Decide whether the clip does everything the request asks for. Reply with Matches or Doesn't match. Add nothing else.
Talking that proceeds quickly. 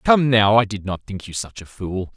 Matches